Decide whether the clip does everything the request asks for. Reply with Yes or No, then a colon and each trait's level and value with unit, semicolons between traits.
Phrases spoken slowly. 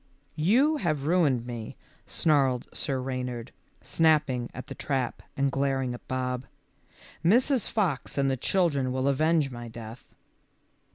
Yes: slow, 130 wpm